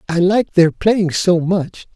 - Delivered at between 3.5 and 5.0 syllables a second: Yes, 4.1 syllables/s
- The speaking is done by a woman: No, male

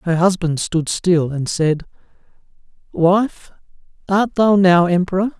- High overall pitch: No, medium, 180 Hz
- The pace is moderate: No, slow, 120 wpm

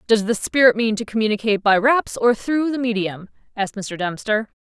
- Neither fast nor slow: Yes, average, 195 wpm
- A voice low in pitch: No, high, 220 Hz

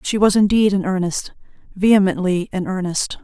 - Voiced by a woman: Yes, female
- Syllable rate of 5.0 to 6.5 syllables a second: Yes, 5.2 syllables/s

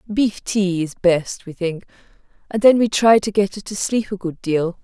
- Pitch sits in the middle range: No, high, 195 Hz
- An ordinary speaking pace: No, fast, 225 wpm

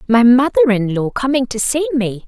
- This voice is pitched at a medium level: No, very high, 250 Hz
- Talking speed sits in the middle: No, fast, 210 wpm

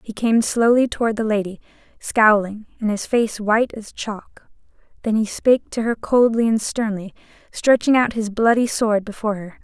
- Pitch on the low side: No, high, 220 Hz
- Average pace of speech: Yes, average, 175 wpm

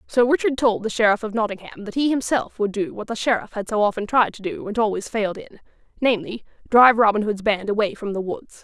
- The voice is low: No, high, 220 Hz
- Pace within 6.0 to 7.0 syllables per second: Yes, 6.2 syllables/s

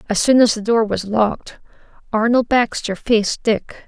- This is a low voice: No, high, 220 Hz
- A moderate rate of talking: Yes, average, 170 wpm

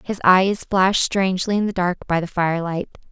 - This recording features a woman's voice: Yes, female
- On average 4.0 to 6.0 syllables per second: Yes, 5.7 syllables/s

